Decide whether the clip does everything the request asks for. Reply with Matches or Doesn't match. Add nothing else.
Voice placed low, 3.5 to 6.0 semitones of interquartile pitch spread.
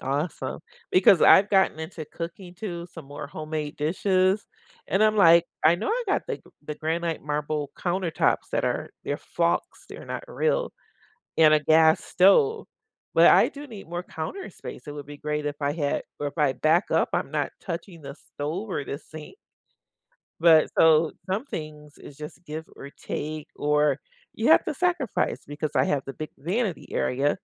Doesn't match